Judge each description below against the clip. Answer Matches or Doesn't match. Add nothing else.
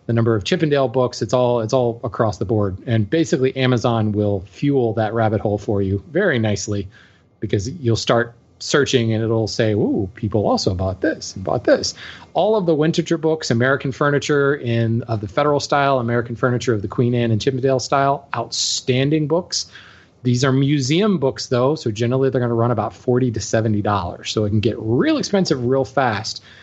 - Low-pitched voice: Matches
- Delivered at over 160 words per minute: Matches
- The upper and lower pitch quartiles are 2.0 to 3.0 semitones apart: Doesn't match